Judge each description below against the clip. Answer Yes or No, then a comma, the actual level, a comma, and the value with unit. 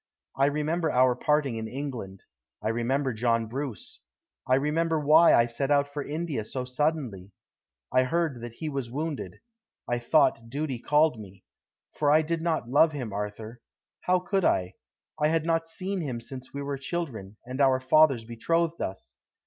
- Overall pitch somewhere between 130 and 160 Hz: Yes, medium, 140 Hz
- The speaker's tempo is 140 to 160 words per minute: No, average, 170 wpm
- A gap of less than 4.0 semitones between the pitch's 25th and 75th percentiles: No, average, 5.0 semitones